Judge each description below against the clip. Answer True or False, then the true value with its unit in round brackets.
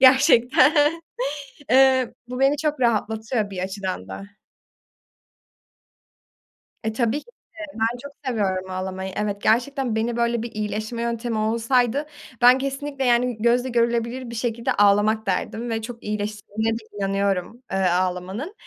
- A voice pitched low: False (230 Hz)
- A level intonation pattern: False (3.3 semitones)